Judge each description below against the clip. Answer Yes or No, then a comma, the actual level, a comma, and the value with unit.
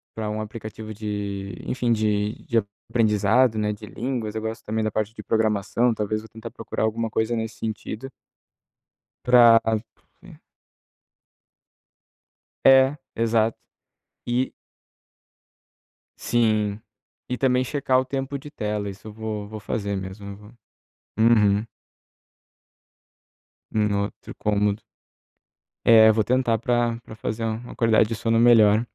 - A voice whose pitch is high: No, low, 110 Hz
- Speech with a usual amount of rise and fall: No, narrow, 1.8 semitones